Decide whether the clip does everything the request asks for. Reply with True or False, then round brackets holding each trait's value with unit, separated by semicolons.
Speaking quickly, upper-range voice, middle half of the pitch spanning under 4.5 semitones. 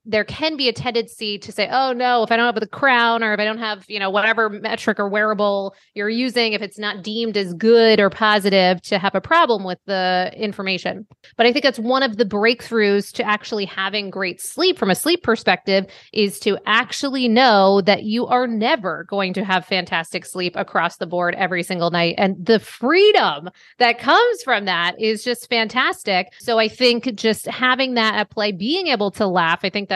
True (210 wpm; 215 Hz; 3.4 semitones)